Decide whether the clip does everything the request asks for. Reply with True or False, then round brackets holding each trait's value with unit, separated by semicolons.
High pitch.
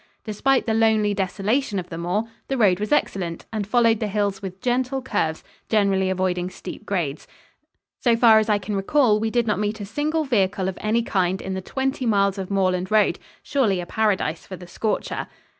True (205 Hz)